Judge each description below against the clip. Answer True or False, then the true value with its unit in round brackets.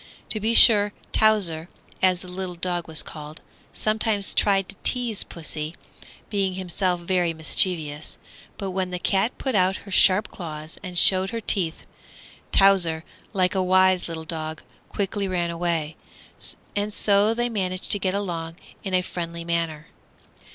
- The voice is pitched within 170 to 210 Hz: True (185 Hz)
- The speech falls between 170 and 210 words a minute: False (150 wpm)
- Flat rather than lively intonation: False (3.0 semitones)